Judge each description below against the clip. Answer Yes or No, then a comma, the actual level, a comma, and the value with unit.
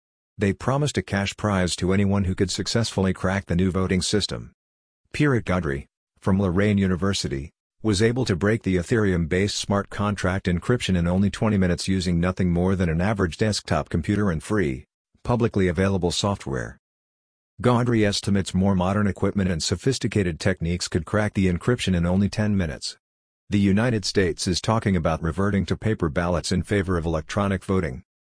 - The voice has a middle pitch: No, very low, 95 Hz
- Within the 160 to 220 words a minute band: Yes, average, 165 wpm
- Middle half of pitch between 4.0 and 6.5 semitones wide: No, narrow, 2.5 semitones